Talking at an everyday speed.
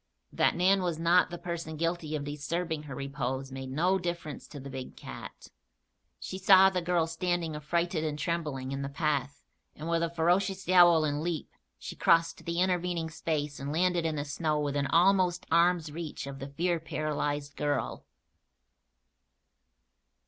Yes: average, 165 wpm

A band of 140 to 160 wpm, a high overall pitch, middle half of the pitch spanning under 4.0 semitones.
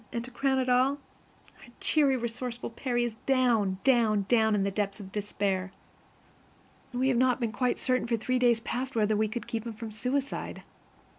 No: average, 180 wpm; high, 235 Hz; average, 3.0 semitones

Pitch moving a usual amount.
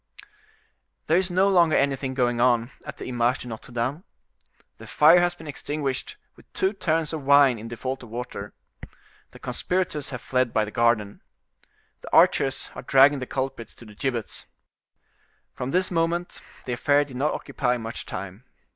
Yes: average, 4.4 semitones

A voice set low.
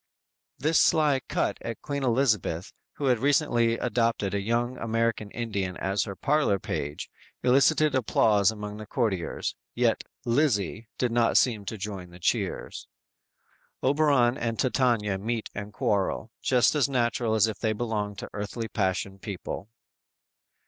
Yes: low, 115 Hz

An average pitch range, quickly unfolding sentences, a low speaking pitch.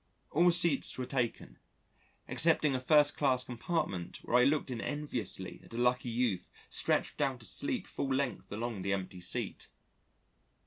No: average, 4.0 semitones; average, 150 wpm; low, 125 Hz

